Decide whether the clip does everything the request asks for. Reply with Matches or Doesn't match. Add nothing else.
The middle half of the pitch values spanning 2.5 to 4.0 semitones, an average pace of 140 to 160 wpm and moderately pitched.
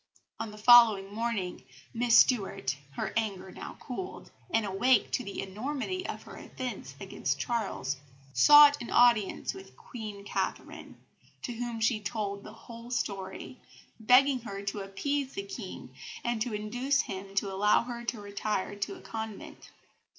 Doesn't match